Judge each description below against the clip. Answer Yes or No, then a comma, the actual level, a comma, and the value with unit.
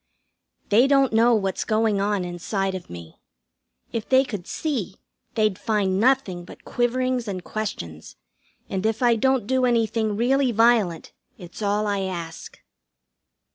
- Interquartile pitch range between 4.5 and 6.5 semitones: No, average, 4.1 semitones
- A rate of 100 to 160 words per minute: Yes, average, 140 wpm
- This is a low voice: No, high, 215 Hz